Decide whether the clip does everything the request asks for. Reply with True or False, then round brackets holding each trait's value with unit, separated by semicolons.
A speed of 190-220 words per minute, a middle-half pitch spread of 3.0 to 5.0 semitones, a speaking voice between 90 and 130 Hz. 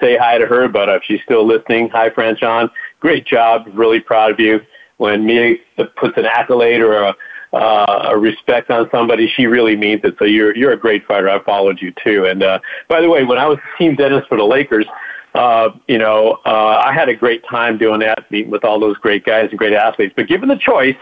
False (230 wpm; 3.5 semitones; 115 Hz)